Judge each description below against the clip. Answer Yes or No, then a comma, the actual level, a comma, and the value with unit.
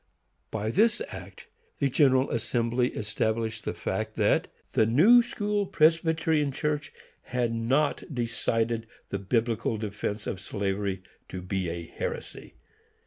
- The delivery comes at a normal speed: No, slow, 125 wpm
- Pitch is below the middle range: Yes, low, 115 Hz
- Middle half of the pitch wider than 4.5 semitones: Yes, wide, 5.6 semitones